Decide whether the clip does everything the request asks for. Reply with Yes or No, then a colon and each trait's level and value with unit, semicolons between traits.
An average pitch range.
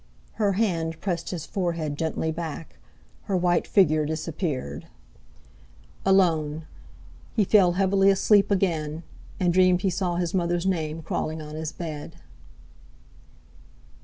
Yes: average, 3.2 semitones